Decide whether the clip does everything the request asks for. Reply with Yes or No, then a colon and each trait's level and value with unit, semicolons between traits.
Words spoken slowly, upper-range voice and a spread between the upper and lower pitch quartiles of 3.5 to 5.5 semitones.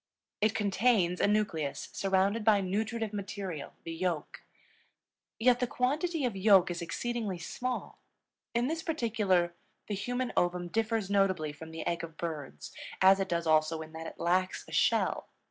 No: average, 160 wpm; high, 195 Hz; average, 4.7 semitones